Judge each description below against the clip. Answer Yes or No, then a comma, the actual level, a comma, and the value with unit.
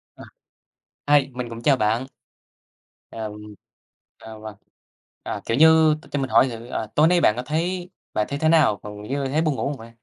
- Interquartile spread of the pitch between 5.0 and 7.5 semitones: Yes, wide, 5.5 semitones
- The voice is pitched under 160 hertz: Yes, low, 135 Hz